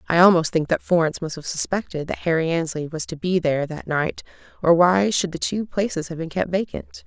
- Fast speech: Yes, fast, 230 wpm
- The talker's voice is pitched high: No, medium, 170 Hz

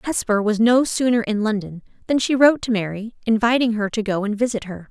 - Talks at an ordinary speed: No, fast, 220 wpm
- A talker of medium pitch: No, high, 220 Hz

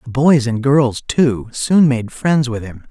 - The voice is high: No, low, 130 Hz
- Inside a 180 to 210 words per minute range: Yes, fast, 205 wpm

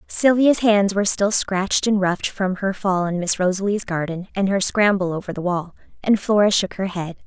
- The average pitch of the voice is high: Yes, high, 195 Hz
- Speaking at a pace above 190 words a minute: Yes, fast, 205 wpm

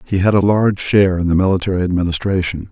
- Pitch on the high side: No, very low, 95 Hz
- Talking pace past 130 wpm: Yes, average, 200 wpm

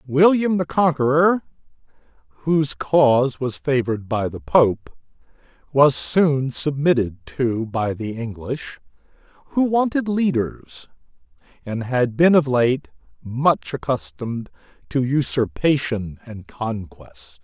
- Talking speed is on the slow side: Yes, slow, 105 wpm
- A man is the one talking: Yes, male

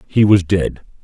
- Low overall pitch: Yes, very low, 95 Hz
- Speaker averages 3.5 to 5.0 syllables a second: Yes, 4.2 syllables/s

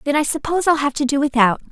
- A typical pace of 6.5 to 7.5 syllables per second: Yes, 7.2 syllables/s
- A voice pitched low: No, very high, 285 Hz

